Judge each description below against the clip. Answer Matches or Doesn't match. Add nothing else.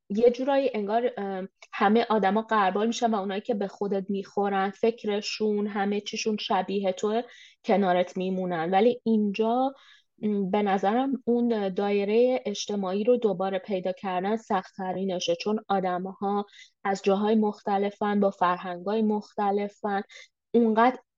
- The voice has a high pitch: Matches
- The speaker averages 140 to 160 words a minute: Doesn't match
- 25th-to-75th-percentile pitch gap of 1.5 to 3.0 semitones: Matches